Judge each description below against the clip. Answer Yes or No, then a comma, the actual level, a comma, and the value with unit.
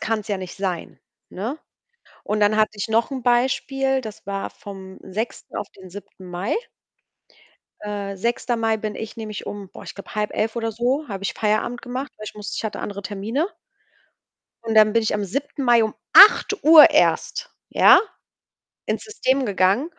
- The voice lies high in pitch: Yes, high, 215 Hz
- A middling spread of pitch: Yes, average, 3.3 semitones